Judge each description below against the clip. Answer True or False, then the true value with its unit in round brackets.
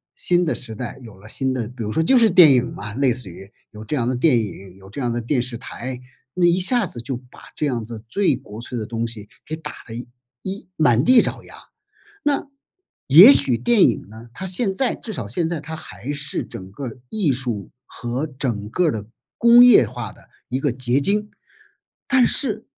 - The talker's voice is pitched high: False (130 Hz)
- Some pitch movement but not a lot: False (7.1 semitones)